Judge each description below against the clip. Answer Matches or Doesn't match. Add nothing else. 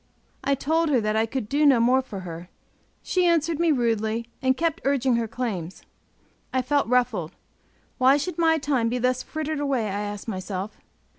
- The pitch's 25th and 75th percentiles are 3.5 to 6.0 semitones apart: Matches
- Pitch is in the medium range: Doesn't match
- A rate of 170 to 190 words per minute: Matches